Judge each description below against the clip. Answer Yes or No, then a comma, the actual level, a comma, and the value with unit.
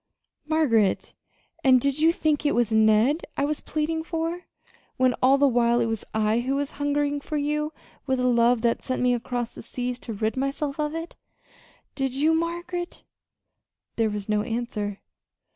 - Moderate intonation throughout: Yes, average, 4.3 semitones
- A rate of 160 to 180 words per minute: Yes, average, 175 wpm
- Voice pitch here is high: Yes, very high, 265 Hz